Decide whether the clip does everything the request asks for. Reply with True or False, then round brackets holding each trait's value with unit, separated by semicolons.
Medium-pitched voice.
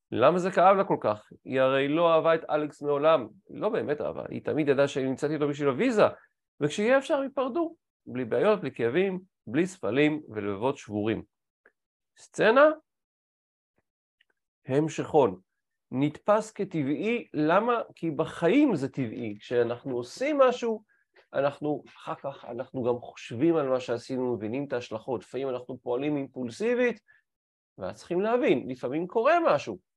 True (150 Hz)